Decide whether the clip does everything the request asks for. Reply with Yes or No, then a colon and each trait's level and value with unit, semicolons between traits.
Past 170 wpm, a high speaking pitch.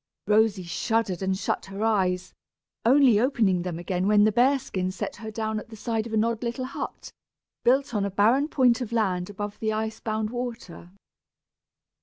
Yes: average, 185 wpm; high, 215 Hz